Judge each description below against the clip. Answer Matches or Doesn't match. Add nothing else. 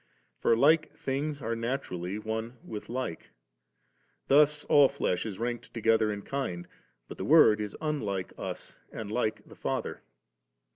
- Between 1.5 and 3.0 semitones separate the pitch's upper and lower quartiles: Doesn't match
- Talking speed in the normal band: Matches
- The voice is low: Matches